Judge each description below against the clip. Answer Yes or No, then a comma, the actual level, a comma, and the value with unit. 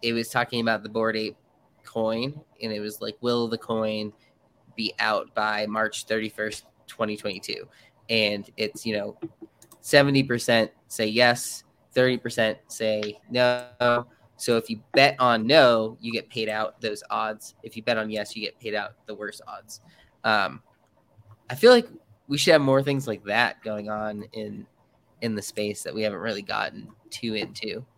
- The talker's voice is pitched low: Yes, low, 110 Hz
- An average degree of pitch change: No, narrow, 2.0 semitones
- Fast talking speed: No, average, 180 wpm